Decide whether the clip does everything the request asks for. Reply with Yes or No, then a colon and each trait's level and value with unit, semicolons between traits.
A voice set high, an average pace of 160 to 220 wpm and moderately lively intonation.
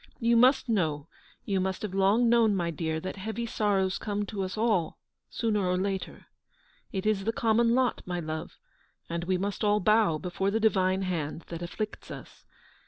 Yes: high, 195 Hz; average, 180 wpm; average, 3.3 semitones